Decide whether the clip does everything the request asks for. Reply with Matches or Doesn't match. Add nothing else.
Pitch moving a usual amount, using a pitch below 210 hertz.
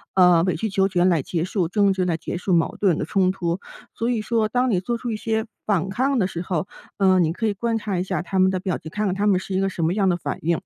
Matches